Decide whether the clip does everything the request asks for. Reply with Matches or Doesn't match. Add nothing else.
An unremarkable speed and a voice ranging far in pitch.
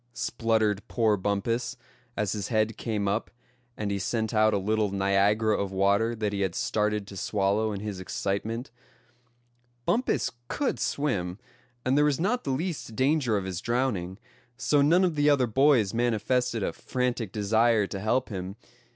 Doesn't match